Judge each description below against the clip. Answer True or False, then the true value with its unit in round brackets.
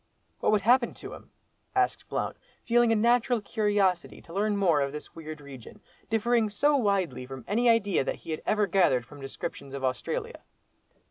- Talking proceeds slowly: False (180 wpm)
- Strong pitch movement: True (7.5 semitones)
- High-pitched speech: True (200 Hz)